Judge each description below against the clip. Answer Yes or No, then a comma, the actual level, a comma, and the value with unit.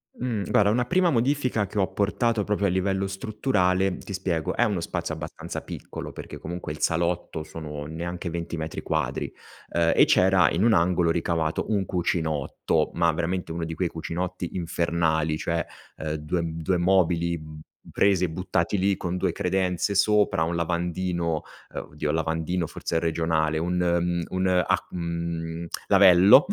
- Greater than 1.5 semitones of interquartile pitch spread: Yes, narrow, 2.5 semitones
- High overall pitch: No, very low, 85 Hz